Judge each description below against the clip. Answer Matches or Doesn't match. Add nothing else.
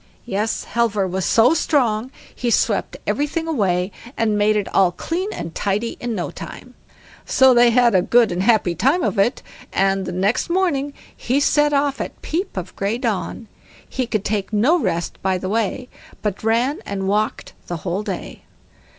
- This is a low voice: Doesn't match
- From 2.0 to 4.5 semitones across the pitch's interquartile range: Doesn't match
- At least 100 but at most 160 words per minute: Doesn't match